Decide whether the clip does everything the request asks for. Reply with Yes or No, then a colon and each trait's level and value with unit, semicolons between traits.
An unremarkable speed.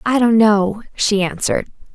Yes: average, 155 wpm